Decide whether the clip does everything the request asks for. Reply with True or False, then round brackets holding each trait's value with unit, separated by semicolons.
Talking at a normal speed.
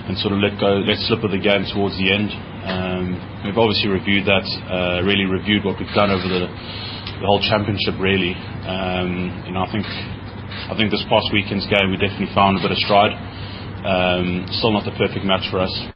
False (210 wpm)